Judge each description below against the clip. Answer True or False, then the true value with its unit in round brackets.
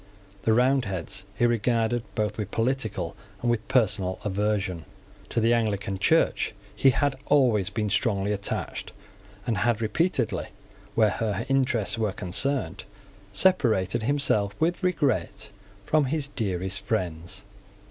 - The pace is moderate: False (125 wpm)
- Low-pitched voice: True (110 Hz)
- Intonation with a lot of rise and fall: False (4.4 semitones)